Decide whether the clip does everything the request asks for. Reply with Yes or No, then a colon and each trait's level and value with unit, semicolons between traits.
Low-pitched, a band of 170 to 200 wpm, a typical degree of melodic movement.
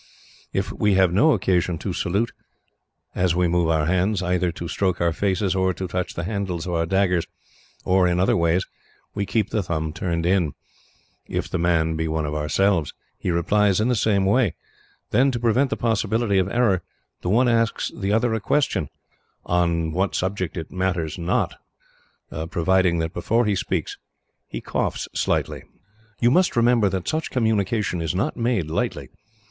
Yes: very low, 95 Hz; average, 175 wpm; average, 3.9 semitones